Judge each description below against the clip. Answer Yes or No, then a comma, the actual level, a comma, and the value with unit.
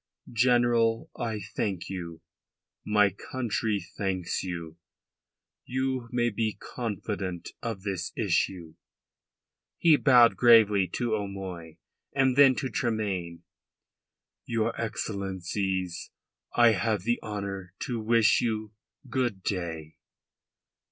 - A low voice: Yes, low, 105 Hz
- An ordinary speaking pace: No, slow, 100 wpm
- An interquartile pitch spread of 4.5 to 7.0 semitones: No, average, 4.0 semitones